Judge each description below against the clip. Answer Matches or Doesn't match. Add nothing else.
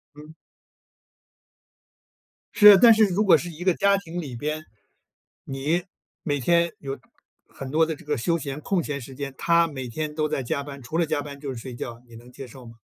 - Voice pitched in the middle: Matches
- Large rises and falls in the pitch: Doesn't match